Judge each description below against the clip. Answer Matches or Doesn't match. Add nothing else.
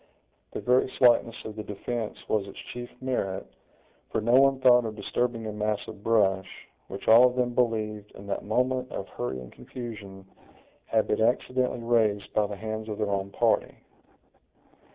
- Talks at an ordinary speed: Matches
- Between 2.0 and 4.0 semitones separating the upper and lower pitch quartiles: Matches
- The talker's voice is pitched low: Matches